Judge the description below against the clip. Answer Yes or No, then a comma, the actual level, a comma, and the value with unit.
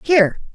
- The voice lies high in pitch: Yes, very high, 250 Hz